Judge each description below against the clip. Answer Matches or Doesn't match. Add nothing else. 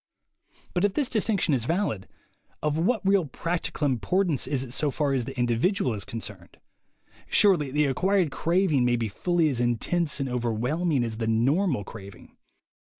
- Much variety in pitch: Matches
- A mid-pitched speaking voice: Matches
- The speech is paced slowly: Doesn't match